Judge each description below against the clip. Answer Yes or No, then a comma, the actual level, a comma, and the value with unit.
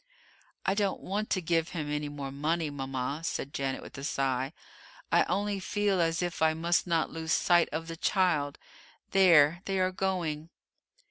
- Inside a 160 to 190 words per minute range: Yes, average, 175 wpm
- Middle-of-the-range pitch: Yes, medium, 165 Hz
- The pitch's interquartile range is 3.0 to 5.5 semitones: Yes, average, 4.0 semitones